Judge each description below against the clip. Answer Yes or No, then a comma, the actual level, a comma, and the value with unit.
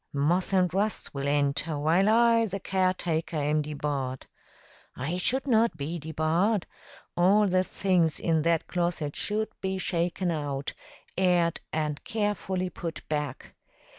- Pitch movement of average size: Yes, average, 3.9 semitones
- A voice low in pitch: No, medium, 170 Hz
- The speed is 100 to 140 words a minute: Yes, slow, 135 wpm